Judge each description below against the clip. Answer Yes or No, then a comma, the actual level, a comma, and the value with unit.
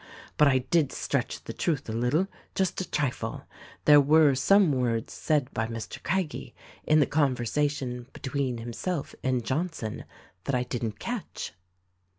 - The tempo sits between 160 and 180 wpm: No, average, 150 wpm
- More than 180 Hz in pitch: No, medium, 140 Hz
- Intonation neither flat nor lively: Yes, average, 4.0 semitones